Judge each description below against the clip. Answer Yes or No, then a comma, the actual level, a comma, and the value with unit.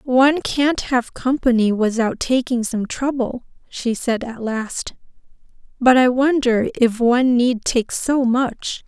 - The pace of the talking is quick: No, average, 140 wpm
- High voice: Yes, high, 245 Hz